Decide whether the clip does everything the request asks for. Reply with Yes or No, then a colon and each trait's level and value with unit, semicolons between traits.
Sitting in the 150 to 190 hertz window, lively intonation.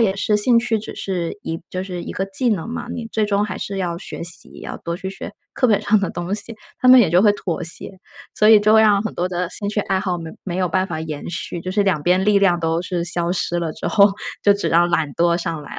No: medium, 185 Hz; average, 3.2 semitones